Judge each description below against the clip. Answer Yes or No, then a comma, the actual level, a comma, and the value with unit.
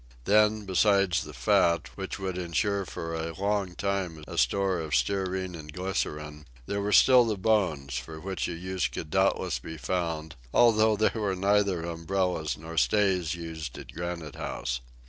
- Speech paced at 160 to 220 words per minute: Yes, average, 165 wpm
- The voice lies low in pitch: Yes, very low, 90 Hz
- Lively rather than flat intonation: No, average, 3.5 semitones